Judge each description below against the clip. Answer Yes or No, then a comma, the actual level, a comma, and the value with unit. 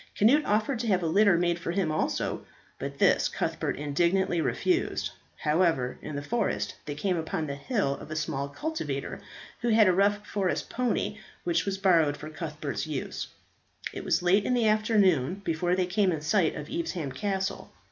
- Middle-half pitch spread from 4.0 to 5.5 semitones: Yes, average, 5.0 semitones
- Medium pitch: Yes, medium, 180 Hz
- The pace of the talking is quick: No, average, 180 wpm